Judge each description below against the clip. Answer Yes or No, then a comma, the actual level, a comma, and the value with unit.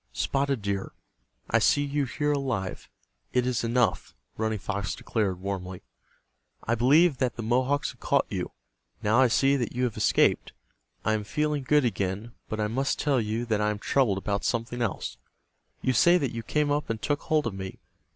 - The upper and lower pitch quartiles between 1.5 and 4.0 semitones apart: No, average, 4.7 semitones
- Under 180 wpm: No, average, 185 wpm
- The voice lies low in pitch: Yes, low, 120 Hz